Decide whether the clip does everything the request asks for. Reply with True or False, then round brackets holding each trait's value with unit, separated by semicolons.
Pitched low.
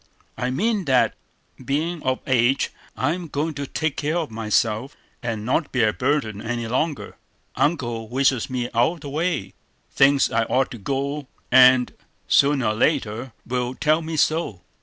True (130 Hz)